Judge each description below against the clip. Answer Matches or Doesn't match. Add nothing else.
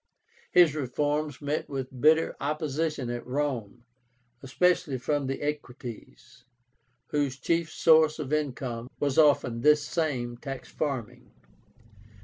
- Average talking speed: Doesn't match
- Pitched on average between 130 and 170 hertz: Matches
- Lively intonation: Doesn't match